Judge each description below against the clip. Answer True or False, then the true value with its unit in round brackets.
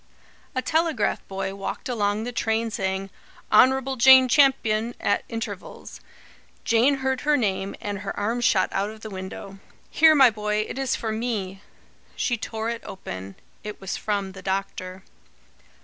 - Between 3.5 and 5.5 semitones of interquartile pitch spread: True (4.1 semitones)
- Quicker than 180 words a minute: False (155 wpm)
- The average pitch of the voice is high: True (215 Hz)